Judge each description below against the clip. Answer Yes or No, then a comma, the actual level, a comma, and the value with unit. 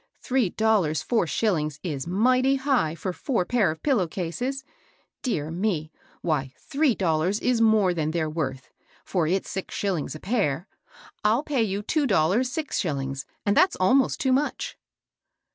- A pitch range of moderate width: No, wide, 7.8 semitones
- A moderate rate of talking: Yes, average, 160 wpm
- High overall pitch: Yes, high, 195 Hz